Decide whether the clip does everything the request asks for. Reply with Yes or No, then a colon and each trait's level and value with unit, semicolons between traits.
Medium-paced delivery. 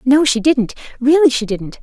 Yes: average, 165 wpm